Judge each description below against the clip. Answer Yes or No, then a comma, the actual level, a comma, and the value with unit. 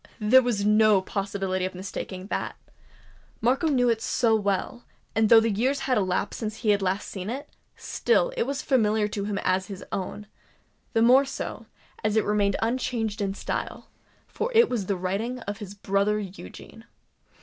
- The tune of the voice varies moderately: Yes, average, 3.4 semitones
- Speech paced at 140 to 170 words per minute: Yes, average, 165 wpm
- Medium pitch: No, high, 210 Hz